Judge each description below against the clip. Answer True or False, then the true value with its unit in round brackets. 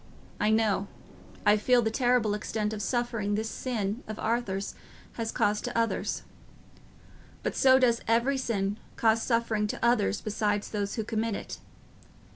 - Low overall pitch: False (220 Hz)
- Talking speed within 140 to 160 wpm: True (150 wpm)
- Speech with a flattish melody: True (2.2 semitones)